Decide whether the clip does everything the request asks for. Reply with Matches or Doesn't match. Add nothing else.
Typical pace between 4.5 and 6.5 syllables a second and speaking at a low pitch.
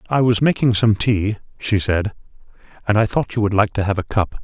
Matches